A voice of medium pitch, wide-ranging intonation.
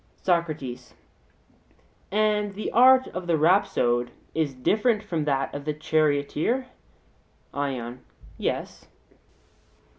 Yes: medium, 155 Hz; wide, 6.8 semitones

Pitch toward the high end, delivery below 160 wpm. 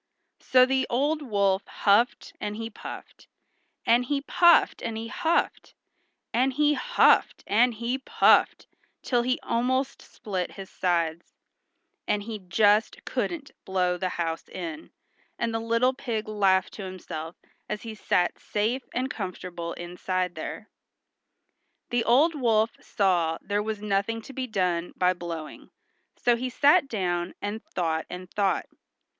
Yes: high, 215 Hz; average, 140 wpm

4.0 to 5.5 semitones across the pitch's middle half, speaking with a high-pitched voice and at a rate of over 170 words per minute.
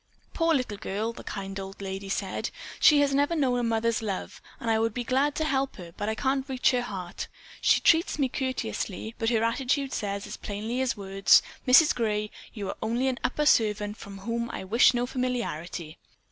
Yes: average, 4.3 semitones; high, 230 Hz; average, 200 wpm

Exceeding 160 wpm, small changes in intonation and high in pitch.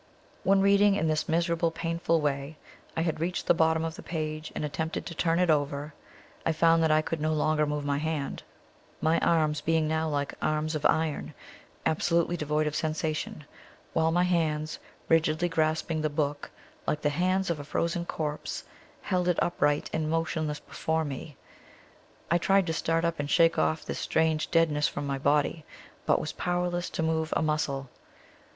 No: average, 180 wpm; narrow, 1.6 semitones; medium, 160 Hz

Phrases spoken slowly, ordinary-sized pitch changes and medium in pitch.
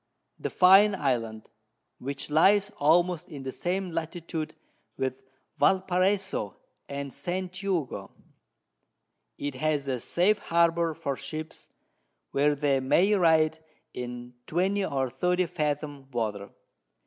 Yes: slow, 115 wpm; average, 4.8 semitones; medium, 155 Hz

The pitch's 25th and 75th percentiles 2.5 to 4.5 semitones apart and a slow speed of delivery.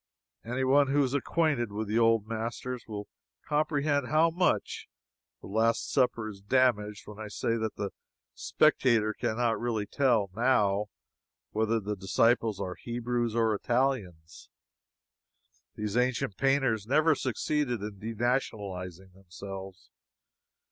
Yes: average, 3.8 semitones; slow, 125 wpm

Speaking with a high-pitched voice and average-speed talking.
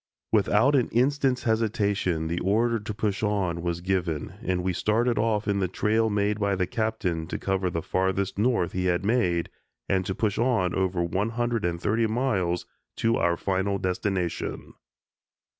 No: low, 100 Hz; average, 170 wpm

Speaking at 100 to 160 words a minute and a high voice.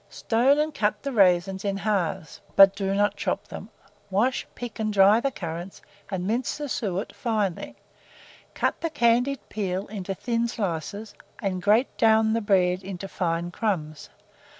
Yes: average, 155 wpm; high, 205 Hz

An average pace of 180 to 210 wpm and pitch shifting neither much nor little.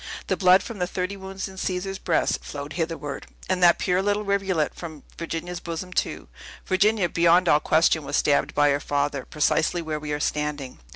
Yes: average, 185 wpm; average, 3.9 semitones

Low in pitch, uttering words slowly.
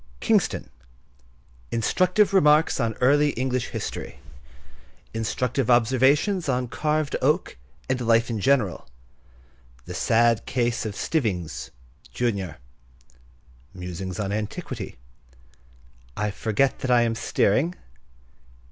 Yes: low, 110 Hz; slow, 80 wpm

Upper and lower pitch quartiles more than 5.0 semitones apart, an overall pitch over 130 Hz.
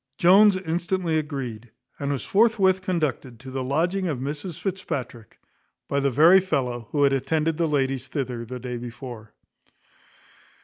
Yes: wide, 5.5 semitones; medium, 140 Hz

